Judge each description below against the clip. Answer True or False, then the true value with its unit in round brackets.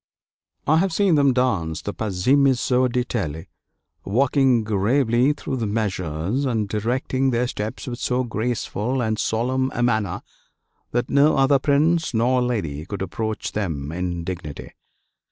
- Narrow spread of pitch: False (4.6 semitones)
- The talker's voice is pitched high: False (120 Hz)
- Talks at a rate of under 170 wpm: True (135 wpm)